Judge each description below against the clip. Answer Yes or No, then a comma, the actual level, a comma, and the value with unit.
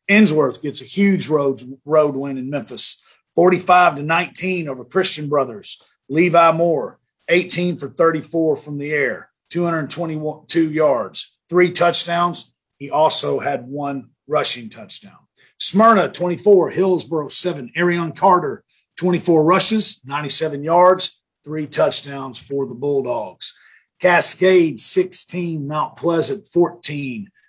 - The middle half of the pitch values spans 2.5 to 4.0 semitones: Yes, average, 3.7 semitones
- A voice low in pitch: No, medium, 165 Hz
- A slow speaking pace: Yes, slow, 115 wpm